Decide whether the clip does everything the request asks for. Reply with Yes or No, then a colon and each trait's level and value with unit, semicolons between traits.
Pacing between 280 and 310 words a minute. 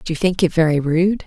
Yes: fast, 285 wpm